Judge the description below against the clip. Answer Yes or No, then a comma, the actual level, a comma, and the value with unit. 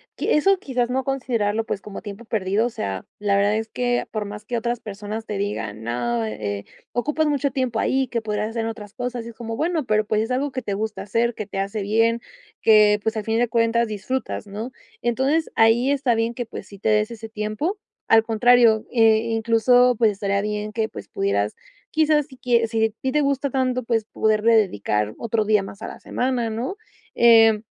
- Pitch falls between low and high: No, high, 225 Hz